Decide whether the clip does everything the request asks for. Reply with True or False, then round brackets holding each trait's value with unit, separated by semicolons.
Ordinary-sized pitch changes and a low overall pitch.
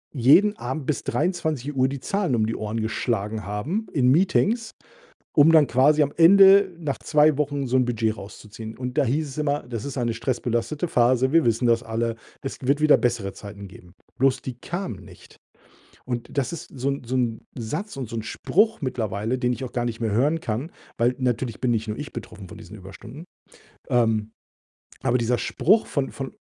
True (4.6 semitones; 125 Hz)